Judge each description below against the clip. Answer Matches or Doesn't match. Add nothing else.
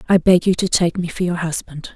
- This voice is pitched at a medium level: Matches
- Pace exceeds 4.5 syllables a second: Matches